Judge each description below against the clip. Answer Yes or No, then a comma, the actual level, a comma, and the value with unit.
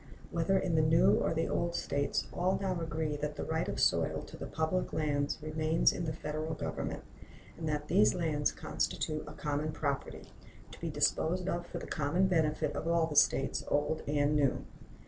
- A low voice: No, medium, 155 Hz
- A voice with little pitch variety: Yes, narrow, 2.2 semitones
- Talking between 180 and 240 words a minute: Yes, average, 190 wpm